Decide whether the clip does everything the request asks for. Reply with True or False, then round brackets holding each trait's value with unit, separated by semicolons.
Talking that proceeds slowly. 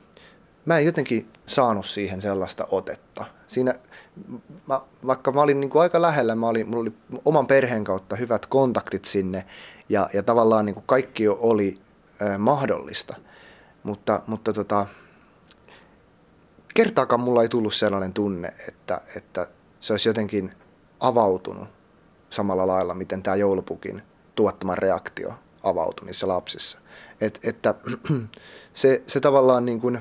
False (135 wpm)